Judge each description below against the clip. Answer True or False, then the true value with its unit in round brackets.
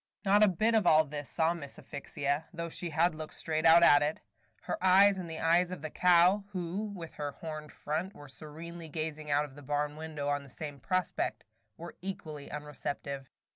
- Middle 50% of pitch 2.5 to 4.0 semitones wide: True (3.0 semitones)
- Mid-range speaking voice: True (160 Hz)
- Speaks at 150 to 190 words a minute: False (200 wpm)